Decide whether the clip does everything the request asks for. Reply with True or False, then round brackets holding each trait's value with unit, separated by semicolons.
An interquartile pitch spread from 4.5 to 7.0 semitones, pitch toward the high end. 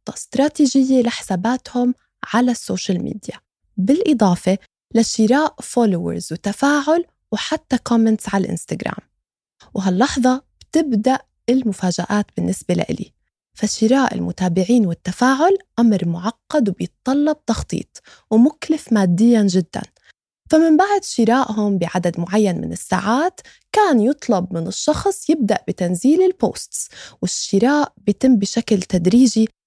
True (5.5 semitones; 230 Hz)